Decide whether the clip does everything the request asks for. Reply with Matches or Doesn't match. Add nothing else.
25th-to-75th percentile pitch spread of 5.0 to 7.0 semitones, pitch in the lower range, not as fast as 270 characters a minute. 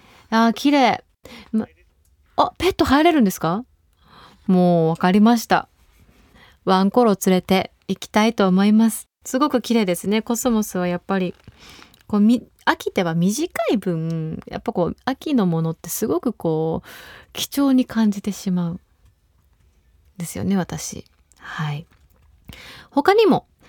Doesn't match